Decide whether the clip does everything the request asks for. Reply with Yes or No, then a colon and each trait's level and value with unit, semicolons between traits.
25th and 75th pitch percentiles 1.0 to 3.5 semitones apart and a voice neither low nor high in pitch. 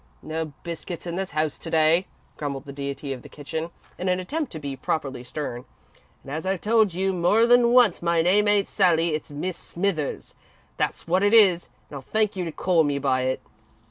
No: average, 4.8 semitones; medium, 170 Hz